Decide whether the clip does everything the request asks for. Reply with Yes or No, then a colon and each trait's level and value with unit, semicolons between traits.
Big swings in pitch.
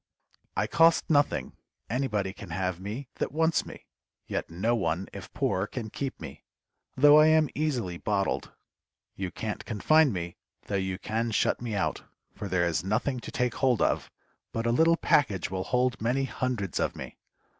Yes: wide, 5.9 semitones